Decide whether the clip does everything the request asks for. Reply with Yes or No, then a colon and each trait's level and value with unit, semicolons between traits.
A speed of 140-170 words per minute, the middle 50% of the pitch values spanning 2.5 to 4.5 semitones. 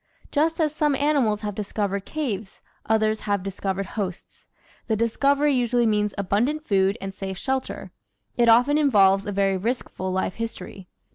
No: average, 150 wpm; average, 5.1 semitones